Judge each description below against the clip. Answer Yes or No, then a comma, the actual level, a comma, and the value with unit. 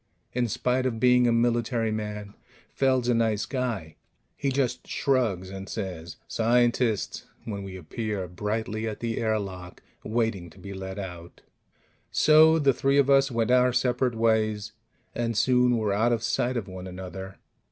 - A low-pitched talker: Yes, low, 115 Hz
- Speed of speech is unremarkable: Yes, average, 160 wpm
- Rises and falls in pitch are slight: No, average, 3.9 semitones